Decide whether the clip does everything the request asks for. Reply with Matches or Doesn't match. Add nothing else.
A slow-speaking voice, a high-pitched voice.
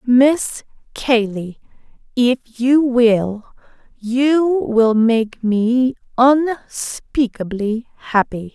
Matches